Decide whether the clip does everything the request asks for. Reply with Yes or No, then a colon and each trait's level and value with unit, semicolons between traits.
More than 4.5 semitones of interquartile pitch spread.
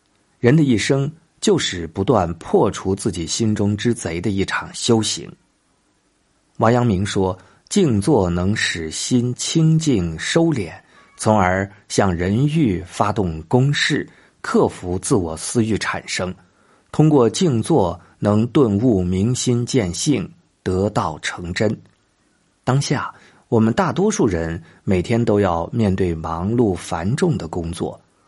Yes: average, 5.3 semitones